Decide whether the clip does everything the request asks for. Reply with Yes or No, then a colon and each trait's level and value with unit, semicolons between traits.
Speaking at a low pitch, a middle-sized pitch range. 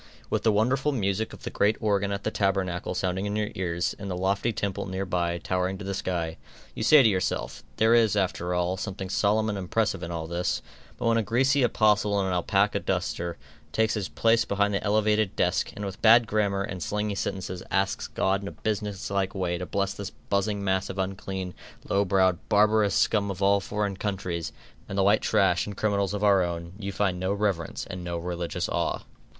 No: low, 100 Hz; narrow, 2.2 semitones